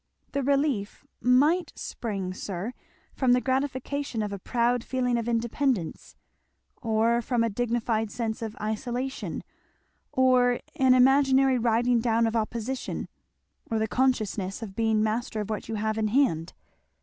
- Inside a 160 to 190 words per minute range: No, average, 140 wpm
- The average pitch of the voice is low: No, high, 235 Hz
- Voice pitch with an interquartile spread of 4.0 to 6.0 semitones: No, average, 2.9 semitones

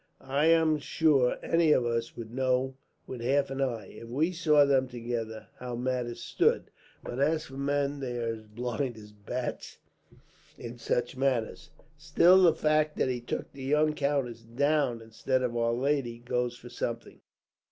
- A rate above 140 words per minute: Yes, average, 170 wpm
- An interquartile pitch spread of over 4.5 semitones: No, average, 3.4 semitones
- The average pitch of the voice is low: Yes, low, 130 Hz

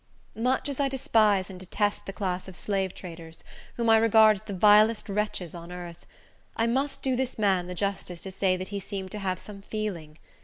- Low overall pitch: No, high, 200 Hz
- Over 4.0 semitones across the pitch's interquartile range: No, average, 3.0 semitones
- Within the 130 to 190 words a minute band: No, fast, 205 wpm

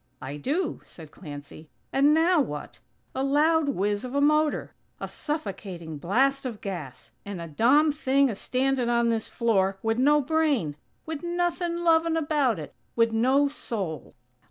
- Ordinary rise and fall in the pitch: No, wide, 7.3 semitones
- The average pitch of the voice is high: Yes, very high, 260 Hz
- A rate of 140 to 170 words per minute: Yes, average, 155 wpm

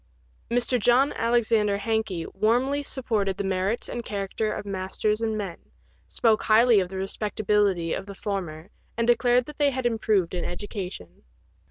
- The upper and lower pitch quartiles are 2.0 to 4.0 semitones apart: Yes, average, 3.6 semitones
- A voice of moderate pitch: No, high, 215 Hz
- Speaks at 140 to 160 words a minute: Yes, average, 150 wpm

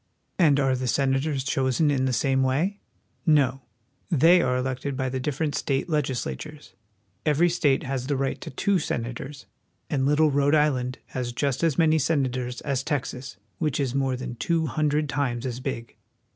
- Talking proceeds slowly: No, average, 170 wpm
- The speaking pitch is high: No, low, 135 Hz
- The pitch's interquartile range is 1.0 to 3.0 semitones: Yes, narrow, 2.6 semitones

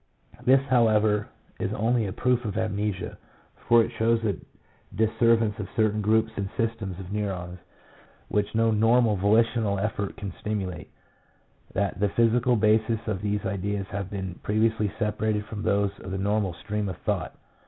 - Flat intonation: Yes, narrow, 2.1 semitones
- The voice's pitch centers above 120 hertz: No, low, 105 Hz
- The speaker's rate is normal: Yes, average, 165 wpm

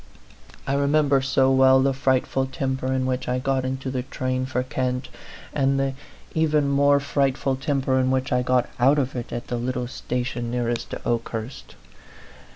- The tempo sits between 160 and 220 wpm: Yes, average, 175 wpm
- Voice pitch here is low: Yes, low, 130 Hz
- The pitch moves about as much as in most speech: No, narrow, 1.3 semitones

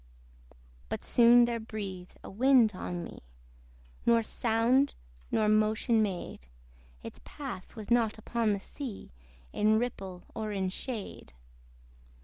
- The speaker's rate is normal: No, slow, 125 wpm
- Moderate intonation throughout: Yes, average, 3.0 semitones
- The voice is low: No, high, 220 Hz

